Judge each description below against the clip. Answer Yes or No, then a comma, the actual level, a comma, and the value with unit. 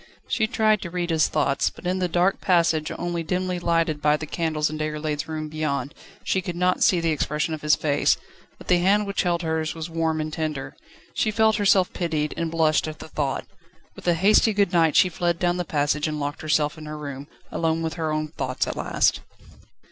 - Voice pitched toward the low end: No, medium, 160 Hz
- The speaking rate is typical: No, fast, 215 wpm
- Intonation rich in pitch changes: No, narrow, 2.6 semitones